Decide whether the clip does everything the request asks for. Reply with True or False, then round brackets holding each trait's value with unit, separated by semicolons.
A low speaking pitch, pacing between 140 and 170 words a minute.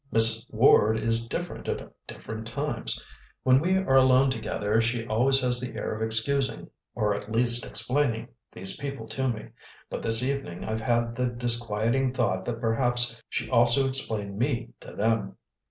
True (115 Hz; 165 wpm)